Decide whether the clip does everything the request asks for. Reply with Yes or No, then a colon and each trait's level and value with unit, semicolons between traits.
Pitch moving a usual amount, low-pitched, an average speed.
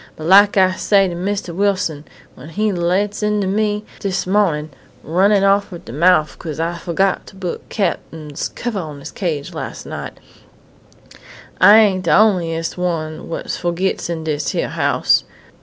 No: average, 3.5 semitones; medium, 185 Hz; average, 160 wpm